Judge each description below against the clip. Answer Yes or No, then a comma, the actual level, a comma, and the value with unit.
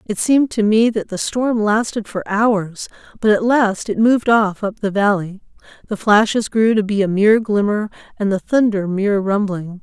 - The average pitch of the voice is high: Yes, high, 210 Hz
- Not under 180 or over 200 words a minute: Yes, average, 195 wpm